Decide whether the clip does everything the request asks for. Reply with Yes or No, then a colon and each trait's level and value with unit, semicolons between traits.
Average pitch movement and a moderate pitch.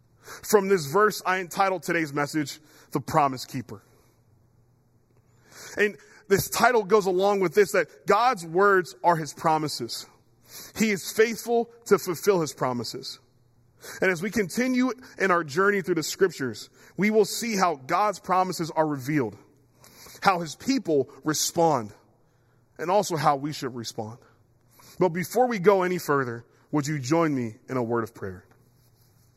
No: wide, 8.0 semitones; medium, 155 Hz